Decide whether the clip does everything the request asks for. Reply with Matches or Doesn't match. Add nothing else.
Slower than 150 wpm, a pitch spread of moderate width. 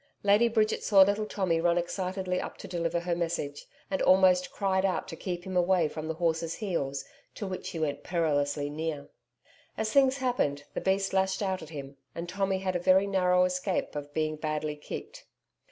Doesn't match